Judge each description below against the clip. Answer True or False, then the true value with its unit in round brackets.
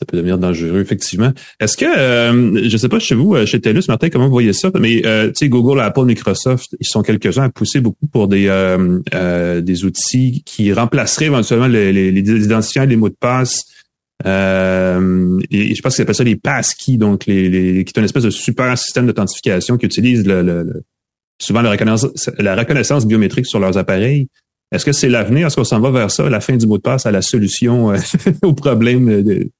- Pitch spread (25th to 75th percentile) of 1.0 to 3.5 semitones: False (4.5 semitones)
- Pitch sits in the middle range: False (110 Hz)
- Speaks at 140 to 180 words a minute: False (215 wpm)